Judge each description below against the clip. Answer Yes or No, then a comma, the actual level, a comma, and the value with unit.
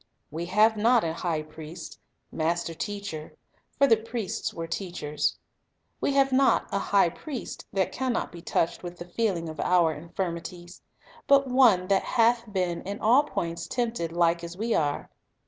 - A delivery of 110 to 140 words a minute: No, average, 180 wpm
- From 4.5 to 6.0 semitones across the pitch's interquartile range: Yes, average, 5.3 semitones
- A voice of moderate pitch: Yes, medium, 180 Hz